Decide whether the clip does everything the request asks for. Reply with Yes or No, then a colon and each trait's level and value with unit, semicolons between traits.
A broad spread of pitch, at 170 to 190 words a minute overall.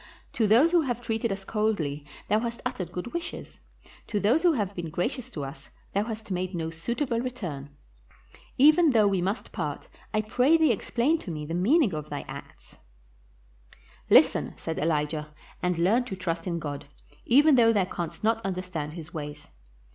Yes: wide, 6.3 semitones; average, 180 wpm